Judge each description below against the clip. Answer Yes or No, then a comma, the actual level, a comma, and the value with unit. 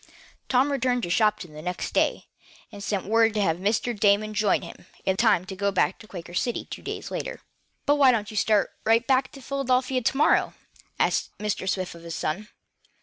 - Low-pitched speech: No, high, 210 Hz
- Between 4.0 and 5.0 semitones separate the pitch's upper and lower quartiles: Yes, average, 4.7 semitones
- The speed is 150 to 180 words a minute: No, fast, 205 wpm